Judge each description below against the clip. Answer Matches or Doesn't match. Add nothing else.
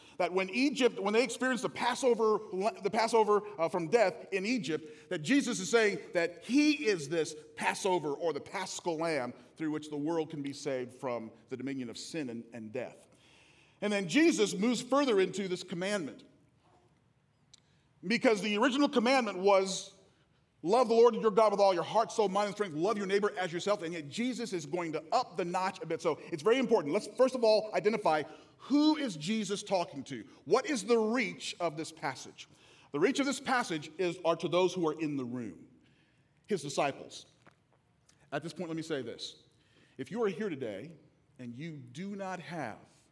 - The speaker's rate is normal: Matches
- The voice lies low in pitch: Doesn't match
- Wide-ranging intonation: Matches